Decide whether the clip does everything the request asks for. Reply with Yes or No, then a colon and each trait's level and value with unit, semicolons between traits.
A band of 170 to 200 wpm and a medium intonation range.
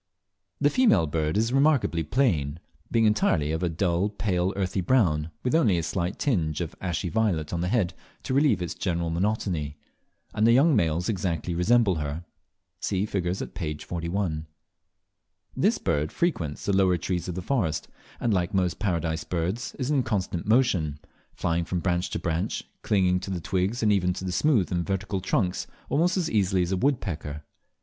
Yes: average, 180 wpm; average, 4.4 semitones